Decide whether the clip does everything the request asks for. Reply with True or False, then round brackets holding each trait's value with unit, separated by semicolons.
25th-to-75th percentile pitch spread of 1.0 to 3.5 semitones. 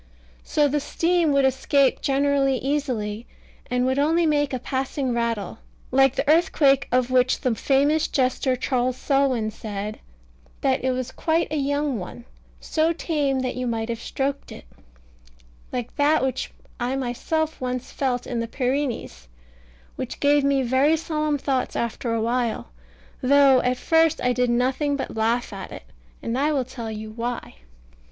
True (2.8 semitones)